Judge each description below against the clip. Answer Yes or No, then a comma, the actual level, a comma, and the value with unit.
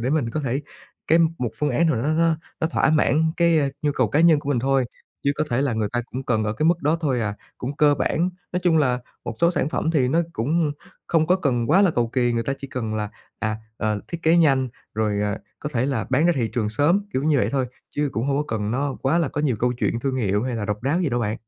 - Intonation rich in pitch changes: No, average, 5.0 semitones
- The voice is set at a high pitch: No, low, 135 Hz